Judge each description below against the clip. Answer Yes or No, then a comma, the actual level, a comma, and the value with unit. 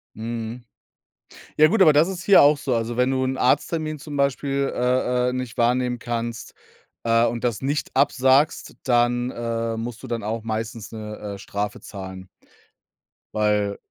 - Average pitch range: Yes, average, 3.0 semitones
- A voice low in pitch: Yes, low, 120 Hz